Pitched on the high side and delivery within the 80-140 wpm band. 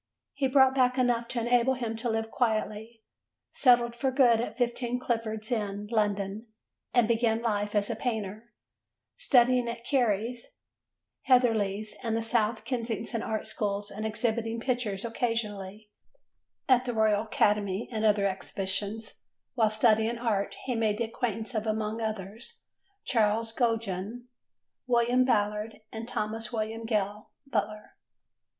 Yes: high, 225 Hz; slow, 135 wpm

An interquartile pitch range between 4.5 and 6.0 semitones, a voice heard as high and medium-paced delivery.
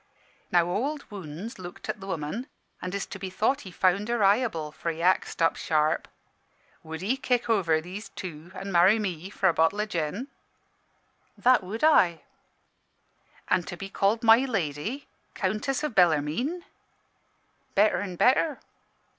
Yes: average, 4.9 semitones; high, 195 Hz; average, 155 wpm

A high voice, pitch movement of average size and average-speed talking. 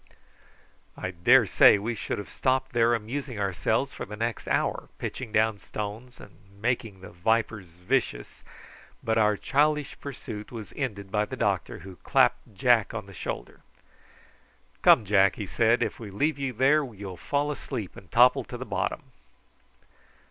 No: low, 110 Hz; average, 4.0 semitones; average, 155 wpm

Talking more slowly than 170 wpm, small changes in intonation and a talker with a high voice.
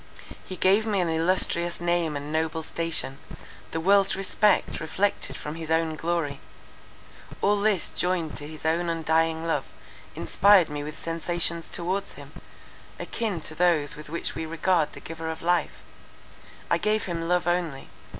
No: average, 155 wpm; narrow, 2.1 semitones; medium, 165 Hz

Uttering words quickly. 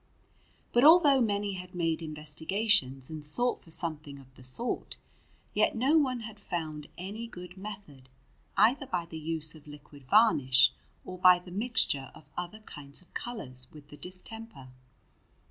No: average, 155 wpm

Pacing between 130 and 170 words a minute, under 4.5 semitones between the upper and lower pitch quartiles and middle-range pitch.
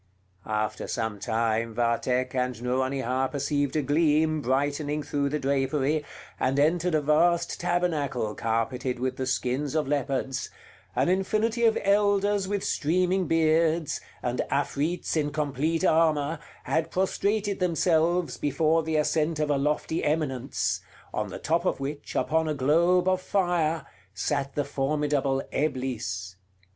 Yes: slow, 135 wpm; average, 3.8 semitones; medium, 150 Hz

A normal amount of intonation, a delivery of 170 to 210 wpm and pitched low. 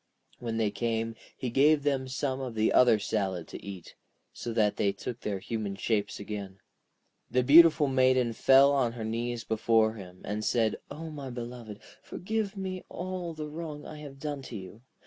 Yes: average, 4.7 semitones; average, 175 wpm; low, 120 Hz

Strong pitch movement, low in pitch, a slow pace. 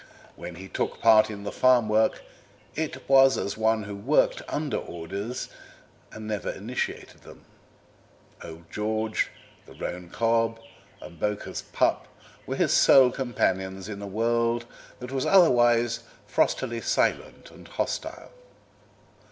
No: average, 3.3 semitones; low, 110 Hz; slow, 130 wpm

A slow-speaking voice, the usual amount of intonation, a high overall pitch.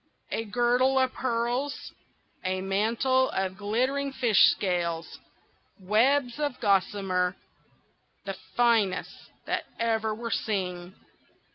Yes: slow, 100 wpm; average, 4.6 semitones; high, 225 Hz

